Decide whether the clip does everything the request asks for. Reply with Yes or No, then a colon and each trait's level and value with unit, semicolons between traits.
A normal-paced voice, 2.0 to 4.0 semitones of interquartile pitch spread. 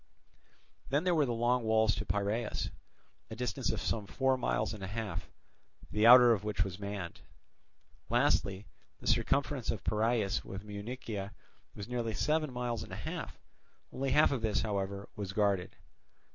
Yes: average, 160 wpm; average, 3.5 semitones